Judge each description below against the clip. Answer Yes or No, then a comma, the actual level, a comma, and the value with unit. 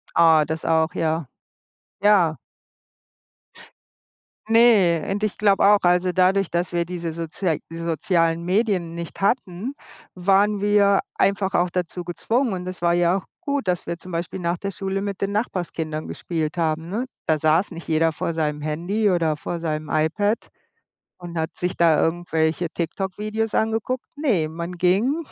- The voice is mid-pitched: Yes, medium, 175 Hz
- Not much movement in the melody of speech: No, average, 3.4 semitones